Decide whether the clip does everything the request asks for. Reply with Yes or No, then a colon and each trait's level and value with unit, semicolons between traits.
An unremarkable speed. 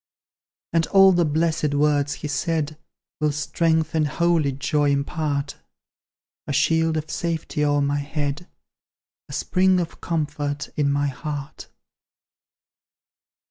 No: slow, 120 wpm